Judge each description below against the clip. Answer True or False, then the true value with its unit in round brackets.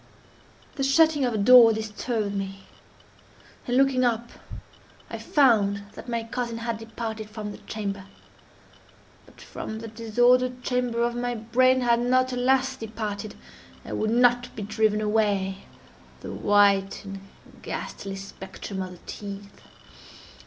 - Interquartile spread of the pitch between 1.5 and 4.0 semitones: True (3.2 semitones)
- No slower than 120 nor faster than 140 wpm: True (135 wpm)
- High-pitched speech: True (225 Hz)